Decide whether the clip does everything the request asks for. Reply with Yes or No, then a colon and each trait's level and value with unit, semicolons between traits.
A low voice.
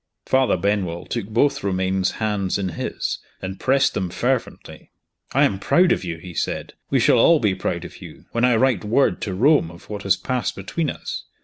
Yes: low, 100 Hz